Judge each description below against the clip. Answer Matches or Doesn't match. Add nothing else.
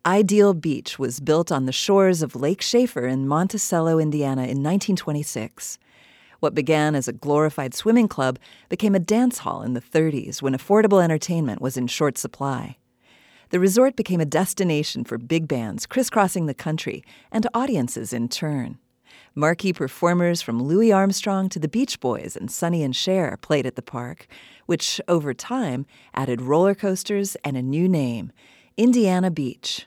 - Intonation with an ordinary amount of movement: Doesn't match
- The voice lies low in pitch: Doesn't match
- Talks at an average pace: Matches